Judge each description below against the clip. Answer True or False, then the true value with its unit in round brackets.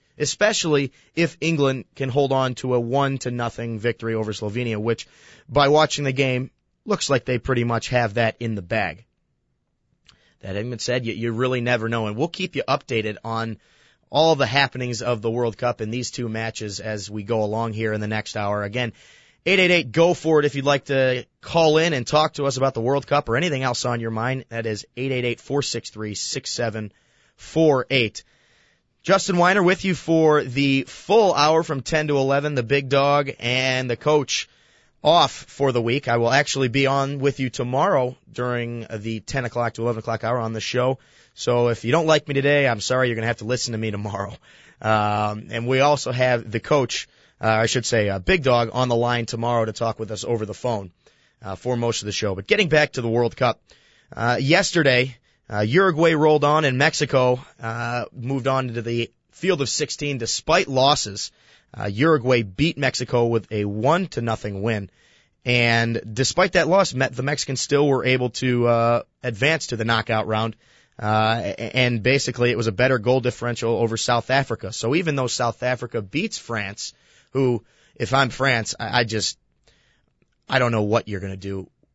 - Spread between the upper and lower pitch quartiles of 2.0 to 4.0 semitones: True (3.4 semitones)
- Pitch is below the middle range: True (125 Hz)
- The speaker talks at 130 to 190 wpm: False (200 wpm)